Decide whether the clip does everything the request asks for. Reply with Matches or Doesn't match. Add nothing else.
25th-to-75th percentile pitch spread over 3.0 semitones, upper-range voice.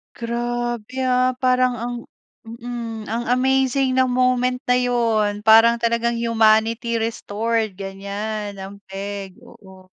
Doesn't match